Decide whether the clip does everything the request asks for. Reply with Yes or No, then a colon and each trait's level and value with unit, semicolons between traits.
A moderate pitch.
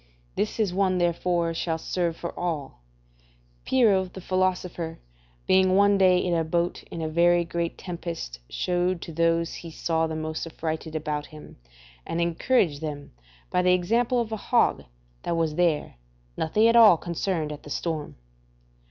Yes: medium, 170 Hz